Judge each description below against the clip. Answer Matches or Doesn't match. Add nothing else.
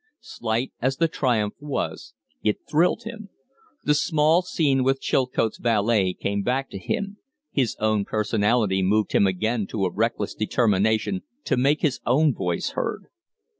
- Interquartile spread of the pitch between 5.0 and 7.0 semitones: Matches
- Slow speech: Doesn't match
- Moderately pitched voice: Doesn't match